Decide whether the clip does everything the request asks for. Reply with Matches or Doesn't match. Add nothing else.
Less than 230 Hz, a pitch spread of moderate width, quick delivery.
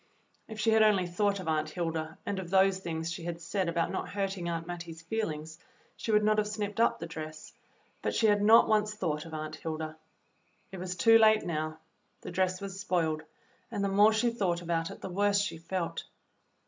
Matches